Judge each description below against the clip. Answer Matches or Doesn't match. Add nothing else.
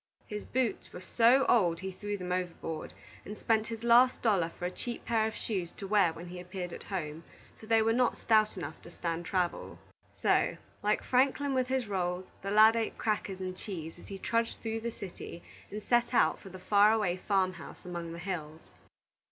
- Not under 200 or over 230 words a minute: Matches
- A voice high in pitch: Matches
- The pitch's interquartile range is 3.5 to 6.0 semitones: Matches